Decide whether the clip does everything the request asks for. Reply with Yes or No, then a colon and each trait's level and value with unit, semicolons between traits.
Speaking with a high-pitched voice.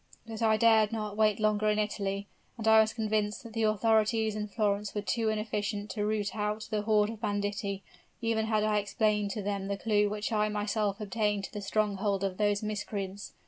Yes: high, 210 Hz